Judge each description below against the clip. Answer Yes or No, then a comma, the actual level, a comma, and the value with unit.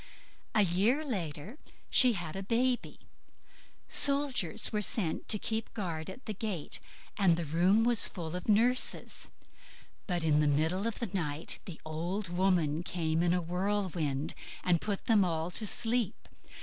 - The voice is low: No, medium, 185 Hz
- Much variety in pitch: No, average, 4.8 semitones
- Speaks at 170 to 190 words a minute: No, average, 155 wpm